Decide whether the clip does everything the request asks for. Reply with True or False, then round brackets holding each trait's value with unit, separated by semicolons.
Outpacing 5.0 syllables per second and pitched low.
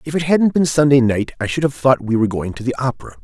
True (6.6 syllables/s; 130 Hz)